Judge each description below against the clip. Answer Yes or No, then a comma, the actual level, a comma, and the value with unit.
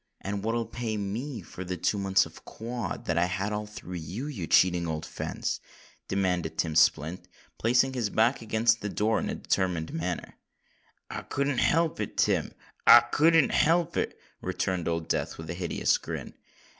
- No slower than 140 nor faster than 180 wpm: Yes, average, 170 wpm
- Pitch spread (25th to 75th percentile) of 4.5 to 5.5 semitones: Yes, average, 5.1 semitones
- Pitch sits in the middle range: No, low, 100 Hz